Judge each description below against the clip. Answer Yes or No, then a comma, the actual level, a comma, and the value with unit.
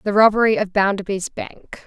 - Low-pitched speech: No, high, 205 Hz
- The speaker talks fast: No, average, 160 wpm